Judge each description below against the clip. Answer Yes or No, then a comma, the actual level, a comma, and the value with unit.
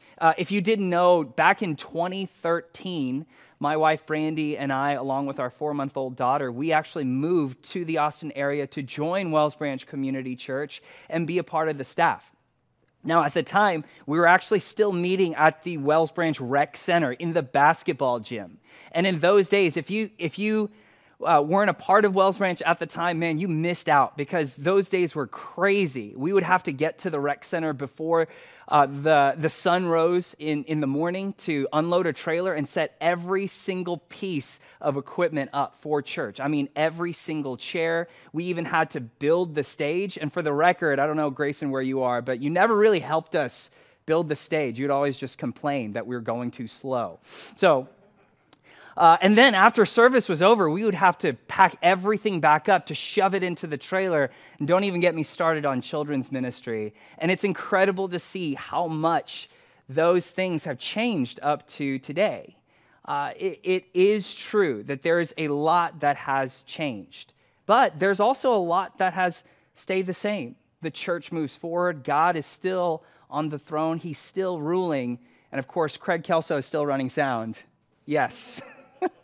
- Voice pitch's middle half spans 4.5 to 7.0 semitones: No, average, 4.1 semitones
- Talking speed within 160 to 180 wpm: No, average, 195 wpm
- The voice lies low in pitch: No, medium, 160 Hz